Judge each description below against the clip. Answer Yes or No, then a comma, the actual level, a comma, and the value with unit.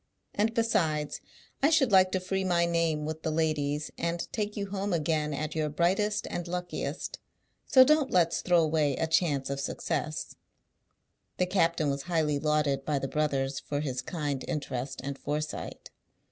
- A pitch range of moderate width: Yes, average, 3.6 semitones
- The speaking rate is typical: Yes, average, 165 wpm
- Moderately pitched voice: Yes, medium, 160 Hz